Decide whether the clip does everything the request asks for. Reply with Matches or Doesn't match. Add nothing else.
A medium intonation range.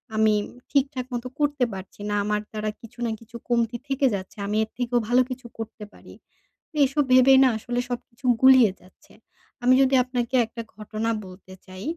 Matches